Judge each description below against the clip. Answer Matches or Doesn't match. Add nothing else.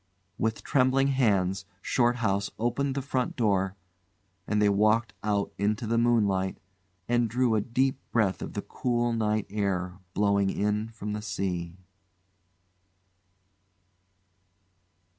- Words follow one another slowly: Matches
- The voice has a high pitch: Doesn't match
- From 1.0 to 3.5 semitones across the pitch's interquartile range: Matches